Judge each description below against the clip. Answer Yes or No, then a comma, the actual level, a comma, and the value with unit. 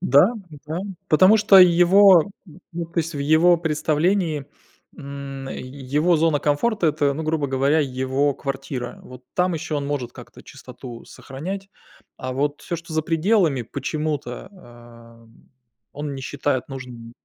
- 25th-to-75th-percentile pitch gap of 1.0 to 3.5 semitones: No, average, 4.0 semitones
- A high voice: No, medium, 150 Hz